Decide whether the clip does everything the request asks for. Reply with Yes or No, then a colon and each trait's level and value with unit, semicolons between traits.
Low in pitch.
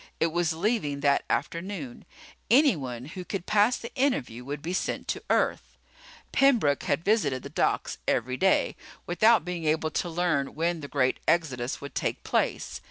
No: medium, 165 Hz